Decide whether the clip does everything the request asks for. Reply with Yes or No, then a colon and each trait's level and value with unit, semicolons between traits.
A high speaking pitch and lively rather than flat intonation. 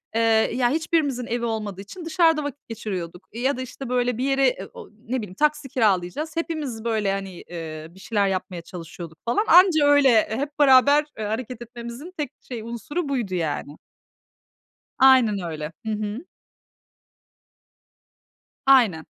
Yes: high, 235 Hz; wide, 5.9 semitones